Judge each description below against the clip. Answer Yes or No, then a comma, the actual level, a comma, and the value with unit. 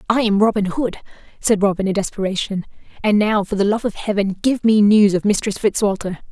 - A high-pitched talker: Yes, high, 205 Hz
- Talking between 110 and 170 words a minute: No, average, 200 wpm